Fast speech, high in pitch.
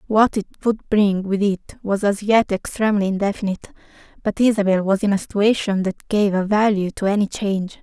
No: average, 185 wpm; high, 200 Hz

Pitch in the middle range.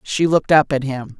Yes: medium, 145 Hz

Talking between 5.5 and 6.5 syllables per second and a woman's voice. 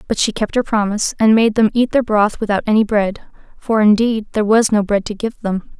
Yes: 5.7 syllables/s; female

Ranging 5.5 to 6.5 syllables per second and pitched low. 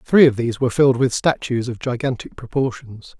Yes: 5.9 syllables/s; low, 125 Hz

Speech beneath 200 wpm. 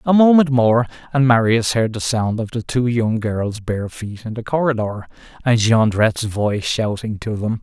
Yes: average, 190 wpm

